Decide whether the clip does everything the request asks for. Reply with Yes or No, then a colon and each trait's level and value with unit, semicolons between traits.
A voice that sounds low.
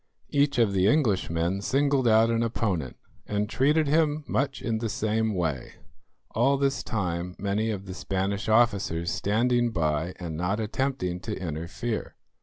Yes: low, 110 Hz